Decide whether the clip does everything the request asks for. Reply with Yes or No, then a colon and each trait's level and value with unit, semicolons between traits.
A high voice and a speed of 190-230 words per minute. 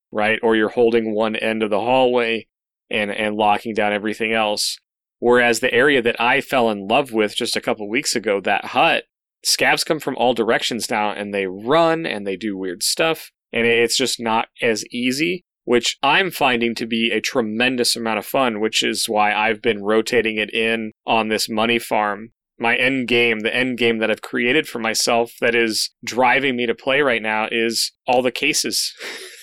No: low, 115 Hz; average, 200 wpm